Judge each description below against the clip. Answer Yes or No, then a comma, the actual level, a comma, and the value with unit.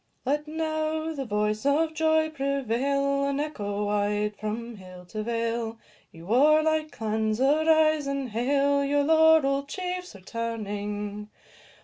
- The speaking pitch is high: Yes, very high, 275 Hz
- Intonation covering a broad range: Yes, wide, 6.3 semitones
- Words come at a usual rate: No, slow, 120 wpm